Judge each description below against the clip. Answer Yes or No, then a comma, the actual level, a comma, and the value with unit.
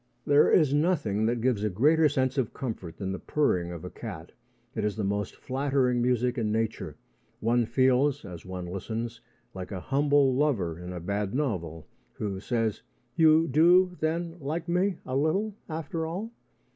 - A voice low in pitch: Yes, low, 125 Hz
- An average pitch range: No, wide, 6.9 semitones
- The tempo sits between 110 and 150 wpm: No, average, 170 wpm